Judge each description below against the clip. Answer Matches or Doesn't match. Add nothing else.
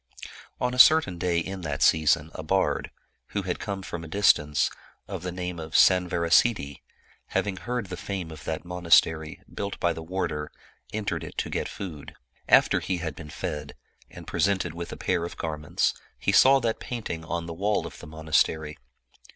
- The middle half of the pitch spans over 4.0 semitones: Doesn't match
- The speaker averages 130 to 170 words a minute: Doesn't match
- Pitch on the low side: Matches